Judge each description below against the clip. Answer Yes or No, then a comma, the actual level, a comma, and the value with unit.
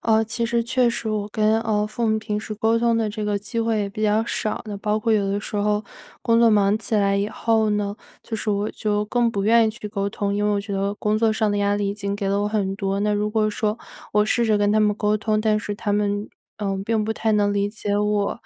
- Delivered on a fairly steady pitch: Yes, narrow, 1.3 semitones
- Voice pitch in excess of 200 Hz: Yes, high, 210 Hz